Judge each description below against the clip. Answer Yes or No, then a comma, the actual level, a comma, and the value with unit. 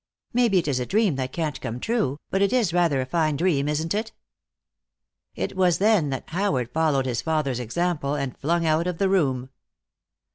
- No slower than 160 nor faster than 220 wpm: Yes, average, 190 wpm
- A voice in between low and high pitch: Yes, medium, 160 Hz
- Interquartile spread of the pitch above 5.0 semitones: Yes, wide, 5.5 semitones